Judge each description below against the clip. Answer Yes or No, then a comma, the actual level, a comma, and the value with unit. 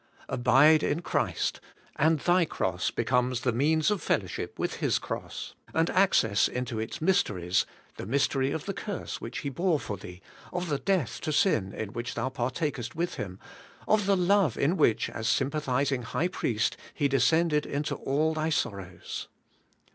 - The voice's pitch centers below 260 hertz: Yes, medium, 140 Hz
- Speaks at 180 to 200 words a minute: No, average, 170 wpm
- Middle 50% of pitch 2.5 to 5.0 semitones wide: No, wide, 5.6 semitones